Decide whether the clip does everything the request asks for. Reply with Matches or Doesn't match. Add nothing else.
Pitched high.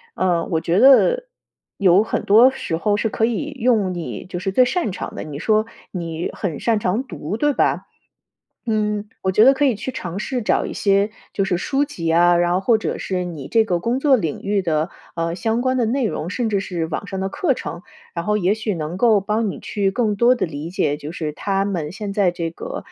Matches